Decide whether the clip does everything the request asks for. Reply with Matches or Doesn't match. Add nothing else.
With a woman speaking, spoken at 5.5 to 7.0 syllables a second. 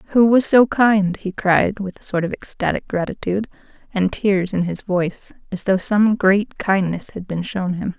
Doesn't match